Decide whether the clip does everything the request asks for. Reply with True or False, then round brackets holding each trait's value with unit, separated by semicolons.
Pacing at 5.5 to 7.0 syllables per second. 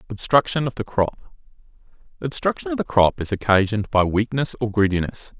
True (5.6 syllables/s)